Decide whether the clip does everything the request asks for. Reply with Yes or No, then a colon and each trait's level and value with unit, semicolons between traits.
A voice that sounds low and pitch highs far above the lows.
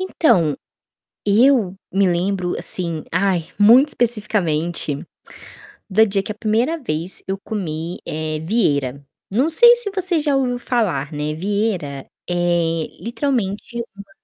No: high, 195 Hz; wide, 6.3 semitones